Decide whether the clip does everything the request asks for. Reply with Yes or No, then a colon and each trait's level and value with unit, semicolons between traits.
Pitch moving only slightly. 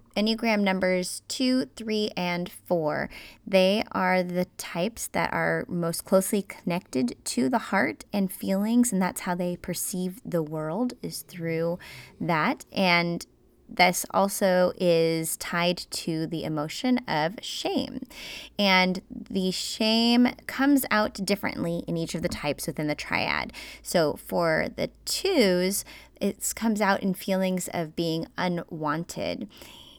No: average, 3.6 semitones